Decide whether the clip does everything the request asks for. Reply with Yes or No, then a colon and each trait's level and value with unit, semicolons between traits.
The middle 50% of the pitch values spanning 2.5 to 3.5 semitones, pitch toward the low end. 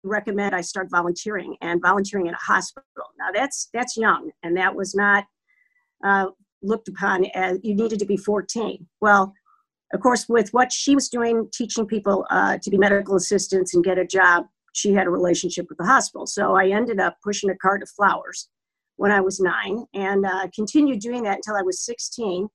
No: average, 2.9 semitones; high, 200 Hz